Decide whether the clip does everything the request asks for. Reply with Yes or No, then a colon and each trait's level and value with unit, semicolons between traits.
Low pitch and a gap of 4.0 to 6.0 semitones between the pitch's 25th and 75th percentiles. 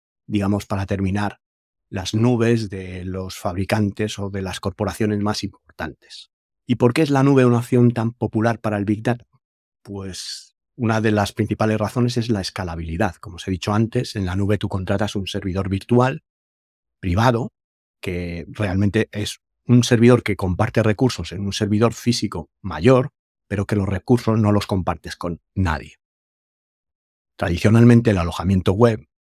No: low, 105 Hz; average, 3.1 semitones